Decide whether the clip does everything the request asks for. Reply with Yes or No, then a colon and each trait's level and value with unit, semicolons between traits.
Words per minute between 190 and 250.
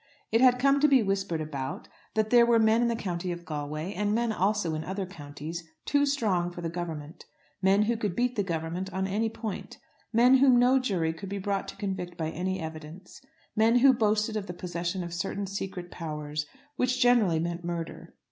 Yes: fast, 205 wpm